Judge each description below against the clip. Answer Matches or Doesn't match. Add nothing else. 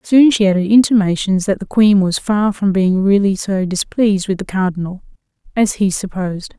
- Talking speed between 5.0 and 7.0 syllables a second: Matches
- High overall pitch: Matches